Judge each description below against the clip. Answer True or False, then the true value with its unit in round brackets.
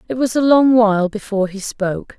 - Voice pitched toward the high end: True (220 Hz)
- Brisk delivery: True (220 wpm)